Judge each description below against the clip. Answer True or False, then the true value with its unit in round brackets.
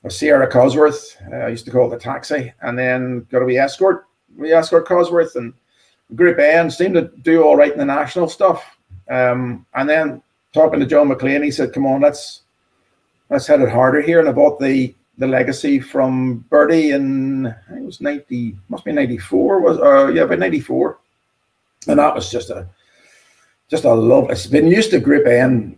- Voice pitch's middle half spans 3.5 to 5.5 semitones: True (4.0 semitones)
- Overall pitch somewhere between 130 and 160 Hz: True (140 Hz)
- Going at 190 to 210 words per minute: True (200 wpm)